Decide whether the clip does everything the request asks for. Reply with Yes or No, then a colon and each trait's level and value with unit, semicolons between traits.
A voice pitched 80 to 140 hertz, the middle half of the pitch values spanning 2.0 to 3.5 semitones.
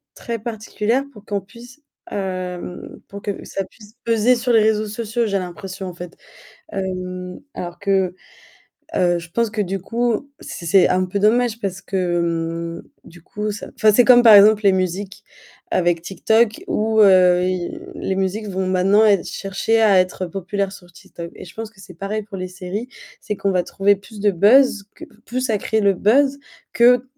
No: high, 200 Hz; average, 3.2 semitones